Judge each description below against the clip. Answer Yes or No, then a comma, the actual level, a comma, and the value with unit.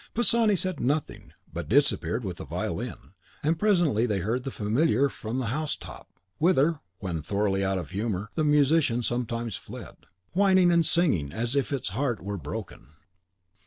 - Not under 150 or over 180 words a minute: Yes, average, 165 wpm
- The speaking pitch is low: Yes, low, 125 Hz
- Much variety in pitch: Yes, wide, 7.2 semitones